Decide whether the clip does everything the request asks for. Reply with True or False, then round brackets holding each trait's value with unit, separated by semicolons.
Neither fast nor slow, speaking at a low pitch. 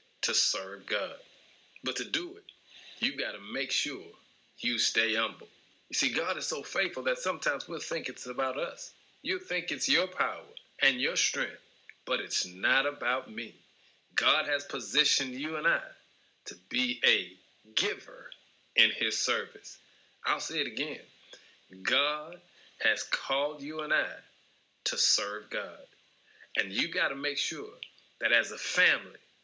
False (155 wpm; 365 Hz)